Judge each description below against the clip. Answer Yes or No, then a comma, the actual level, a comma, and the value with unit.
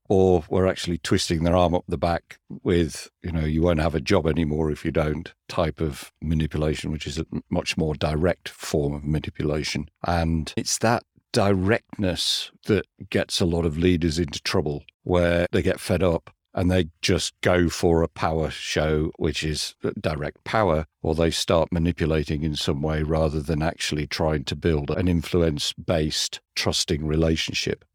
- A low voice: Yes, very low, 80 Hz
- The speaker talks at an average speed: Yes, average, 170 wpm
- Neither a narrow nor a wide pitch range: No, narrow, 2.2 semitones